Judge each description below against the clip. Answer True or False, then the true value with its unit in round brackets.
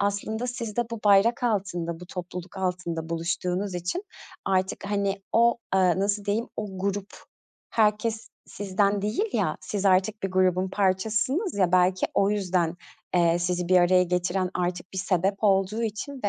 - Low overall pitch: False (195 Hz)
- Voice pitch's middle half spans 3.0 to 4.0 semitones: False (2.5 semitones)